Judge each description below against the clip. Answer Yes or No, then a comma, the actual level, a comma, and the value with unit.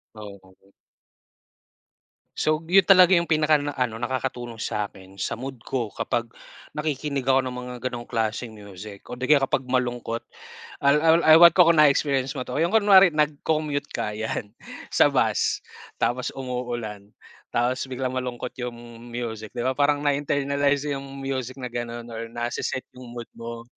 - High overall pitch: No, low, 130 Hz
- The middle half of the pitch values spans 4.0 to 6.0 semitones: No, average, 3.5 semitones